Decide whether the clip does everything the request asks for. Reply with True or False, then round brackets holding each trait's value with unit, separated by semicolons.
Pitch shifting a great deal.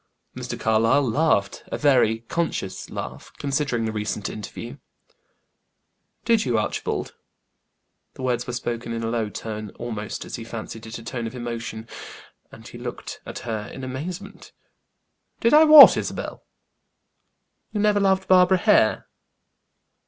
True (6.2 semitones)